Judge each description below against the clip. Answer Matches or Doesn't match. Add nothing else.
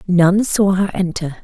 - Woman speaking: Matches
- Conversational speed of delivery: Matches